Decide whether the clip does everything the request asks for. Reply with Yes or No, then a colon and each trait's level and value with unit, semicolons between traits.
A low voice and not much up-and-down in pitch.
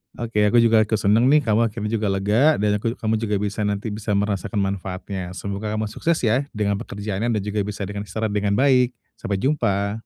Yes: low, 105 Hz; narrow, 2.1 semitones